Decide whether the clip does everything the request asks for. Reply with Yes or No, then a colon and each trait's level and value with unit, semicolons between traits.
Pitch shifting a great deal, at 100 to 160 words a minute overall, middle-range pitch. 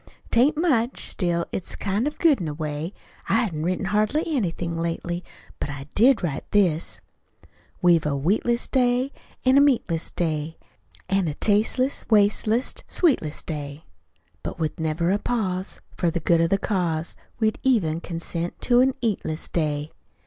Yes: wide, 6.4 semitones; average, 155 wpm; medium, 180 Hz